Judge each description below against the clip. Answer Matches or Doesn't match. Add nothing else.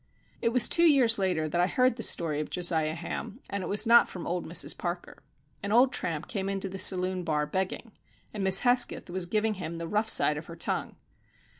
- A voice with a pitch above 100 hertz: Matches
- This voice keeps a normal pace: Doesn't match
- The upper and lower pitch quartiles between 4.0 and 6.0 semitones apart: Matches